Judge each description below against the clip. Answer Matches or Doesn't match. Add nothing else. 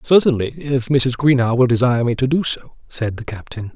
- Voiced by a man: Matches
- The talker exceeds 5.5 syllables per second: Doesn't match